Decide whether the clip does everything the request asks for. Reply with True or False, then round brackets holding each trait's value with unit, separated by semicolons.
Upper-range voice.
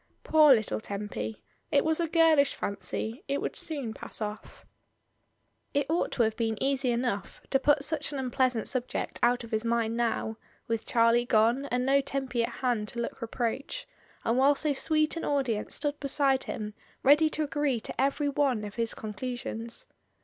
True (250 Hz)